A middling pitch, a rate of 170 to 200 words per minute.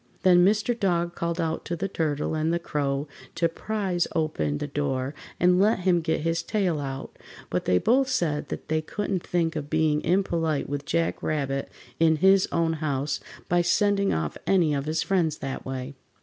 Yes: medium, 165 Hz; average, 185 wpm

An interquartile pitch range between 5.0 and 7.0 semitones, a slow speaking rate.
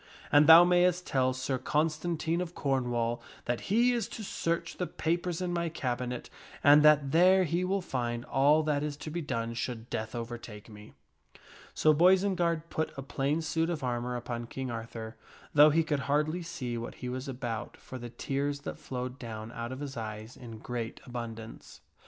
No: wide, 5.4 semitones; average, 180 wpm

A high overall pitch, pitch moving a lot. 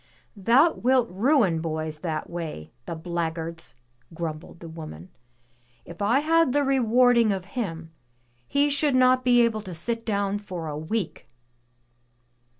Yes: high, 200 Hz; wide, 7.2 semitones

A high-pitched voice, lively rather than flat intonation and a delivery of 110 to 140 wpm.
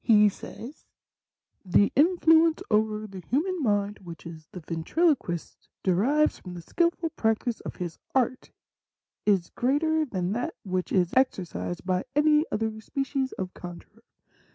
Yes: high, 215 Hz; wide, 8.2 semitones; slow, 135 wpm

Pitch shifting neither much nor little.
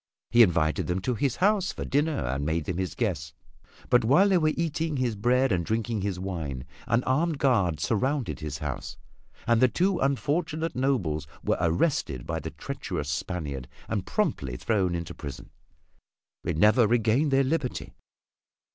No: wide, 8.7 semitones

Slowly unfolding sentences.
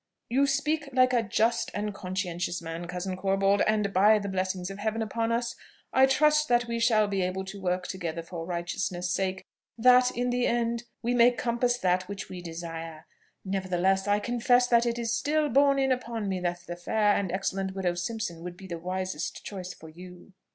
No: average, 200 wpm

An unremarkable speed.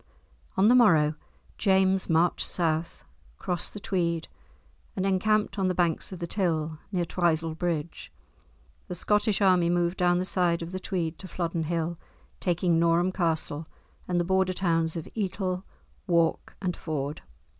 Yes: average, 155 wpm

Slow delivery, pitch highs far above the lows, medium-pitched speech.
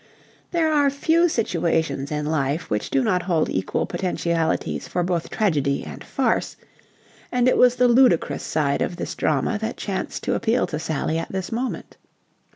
No: average, 165 wpm; wide, 7.8 semitones; medium, 175 Hz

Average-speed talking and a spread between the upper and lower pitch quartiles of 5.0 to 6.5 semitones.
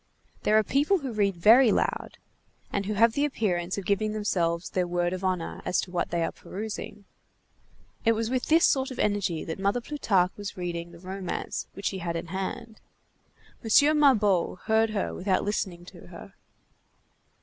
No: average, 180 wpm; average, 3.9 semitones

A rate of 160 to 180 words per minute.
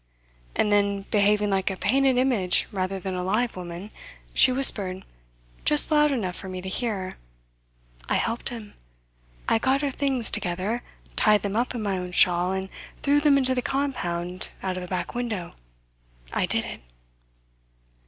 Yes: average, 165 wpm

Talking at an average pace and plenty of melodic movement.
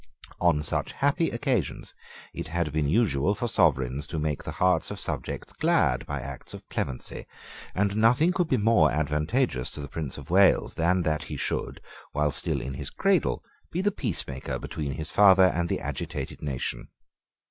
Yes: average, 175 wpm; wide, 7.0 semitones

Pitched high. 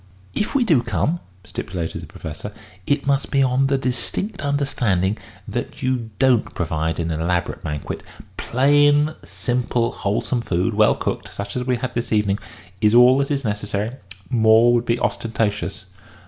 No: low, 120 Hz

